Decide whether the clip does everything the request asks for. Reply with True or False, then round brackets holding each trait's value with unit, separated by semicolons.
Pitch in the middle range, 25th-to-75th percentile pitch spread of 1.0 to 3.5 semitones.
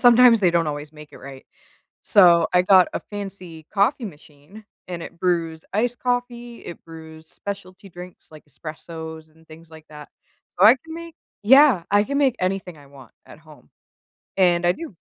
False (175 Hz; 5.0 semitones)